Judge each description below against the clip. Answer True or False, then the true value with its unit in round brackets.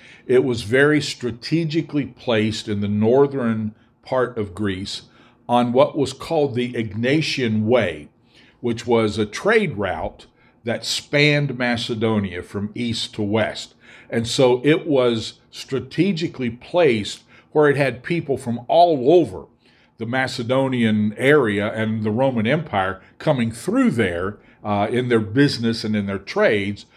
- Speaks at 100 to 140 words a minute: True (135 wpm)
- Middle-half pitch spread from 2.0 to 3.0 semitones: False (4.1 semitones)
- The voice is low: True (120 Hz)